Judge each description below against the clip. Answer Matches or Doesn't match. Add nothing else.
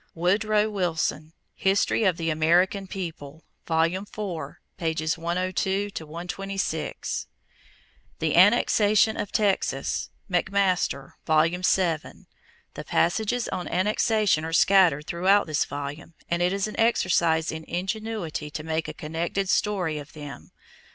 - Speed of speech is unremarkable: Doesn't match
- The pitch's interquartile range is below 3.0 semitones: Doesn't match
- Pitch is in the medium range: Matches